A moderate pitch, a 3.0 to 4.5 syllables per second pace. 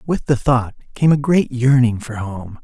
No: low, 125 Hz; 4.4 syllables/s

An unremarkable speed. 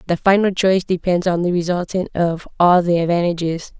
Yes: average, 175 wpm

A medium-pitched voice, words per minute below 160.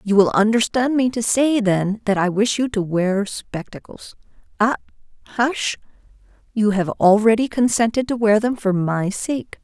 No: high, 215 Hz; average, 150 wpm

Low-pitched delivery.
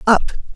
No: high, 220 Hz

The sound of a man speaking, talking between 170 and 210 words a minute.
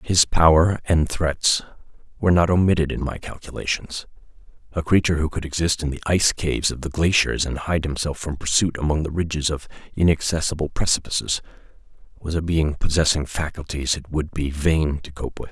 Yes: male; average, 175 wpm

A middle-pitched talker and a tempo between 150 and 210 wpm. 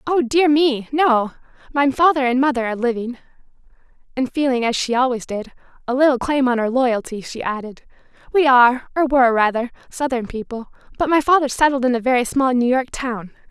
No: very high, 255 Hz; average, 180 wpm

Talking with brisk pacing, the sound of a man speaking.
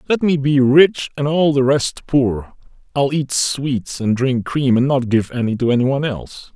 Yes: fast, 210 wpm; male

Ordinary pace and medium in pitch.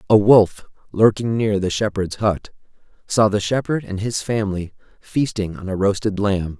No: average, 165 wpm; low, 105 Hz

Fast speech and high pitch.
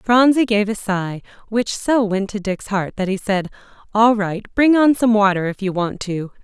Yes: fast, 215 wpm; high, 210 Hz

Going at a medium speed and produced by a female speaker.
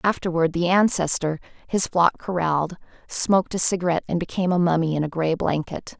Yes: average, 170 wpm; female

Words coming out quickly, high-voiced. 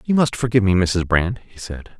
No: fast, 240 wpm; low, 105 Hz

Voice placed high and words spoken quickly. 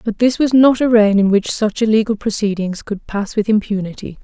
Yes: high, 215 Hz; fast, 210 wpm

